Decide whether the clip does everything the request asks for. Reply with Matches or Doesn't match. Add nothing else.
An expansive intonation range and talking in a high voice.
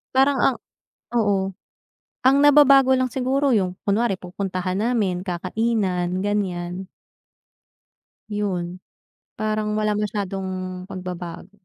Doesn't match